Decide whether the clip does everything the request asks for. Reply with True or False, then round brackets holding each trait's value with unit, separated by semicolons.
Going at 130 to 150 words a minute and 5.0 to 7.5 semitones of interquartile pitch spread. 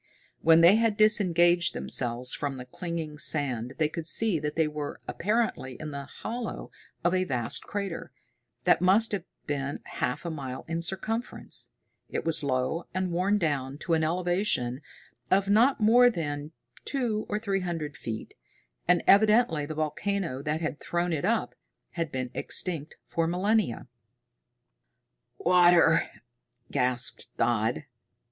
True (140 wpm; 5.3 semitones)